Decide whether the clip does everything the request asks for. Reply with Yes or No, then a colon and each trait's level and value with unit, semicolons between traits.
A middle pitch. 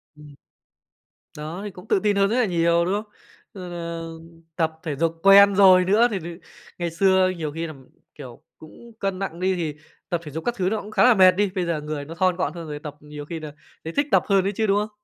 Yes: medium, 180 Hz